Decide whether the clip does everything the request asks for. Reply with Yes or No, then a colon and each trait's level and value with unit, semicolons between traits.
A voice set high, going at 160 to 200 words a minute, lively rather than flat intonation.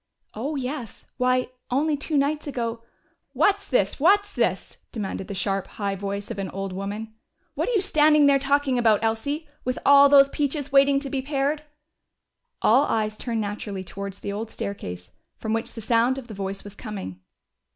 Yes: high, 235 Hz; average, 180 wpm; wide, 5.7 semitones